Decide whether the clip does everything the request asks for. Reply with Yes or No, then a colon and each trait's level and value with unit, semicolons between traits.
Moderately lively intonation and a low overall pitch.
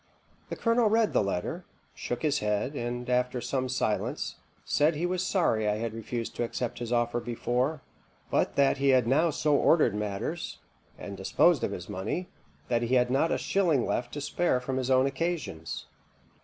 Yes: average, 4.4 semitones; low, 125 Hz